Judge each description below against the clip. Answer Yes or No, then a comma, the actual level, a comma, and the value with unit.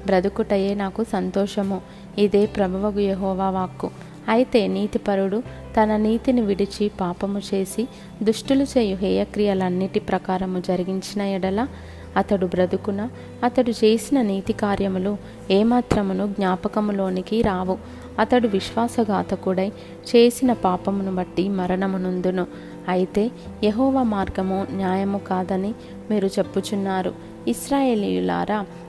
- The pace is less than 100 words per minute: Yes, average, 85 wpm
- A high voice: Yes, high, 200 Hz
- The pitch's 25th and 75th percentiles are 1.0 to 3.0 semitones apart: Yes, narrow, 2.4 semitones